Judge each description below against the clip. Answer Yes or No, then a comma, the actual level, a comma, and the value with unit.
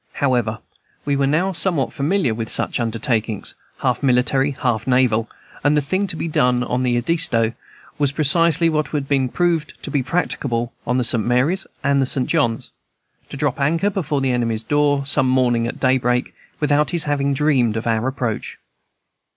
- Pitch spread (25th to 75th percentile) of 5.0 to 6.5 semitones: No, average, 3.6 semitones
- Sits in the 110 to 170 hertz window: Yes, low, 135 Hz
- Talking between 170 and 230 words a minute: Yes, average, 175 wpm